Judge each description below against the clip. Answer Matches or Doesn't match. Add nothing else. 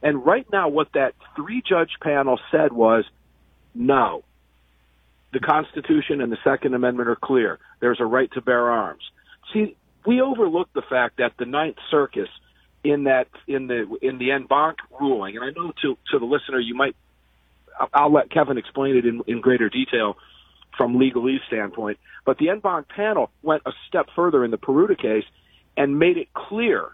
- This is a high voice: Doesn't match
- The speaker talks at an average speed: Matches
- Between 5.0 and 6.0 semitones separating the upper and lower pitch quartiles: Matches